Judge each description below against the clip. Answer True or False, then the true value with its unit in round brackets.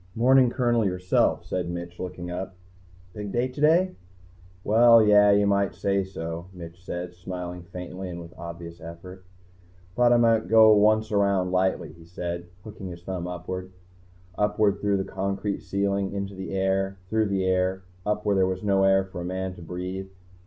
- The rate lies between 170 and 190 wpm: True (175 wpm)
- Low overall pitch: True (95 Hz)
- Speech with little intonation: True (2.3 semitones)